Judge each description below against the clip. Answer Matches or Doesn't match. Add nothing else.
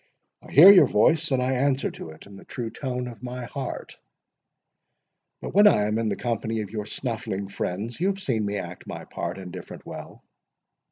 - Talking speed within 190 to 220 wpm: Matches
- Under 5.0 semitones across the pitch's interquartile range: Matches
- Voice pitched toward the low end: Matches